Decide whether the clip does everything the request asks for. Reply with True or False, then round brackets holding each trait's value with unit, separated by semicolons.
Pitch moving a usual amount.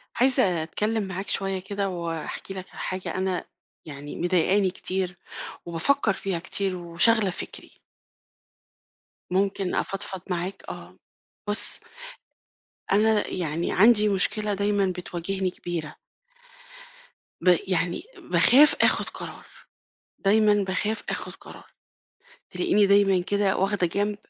False (2.3 semitones)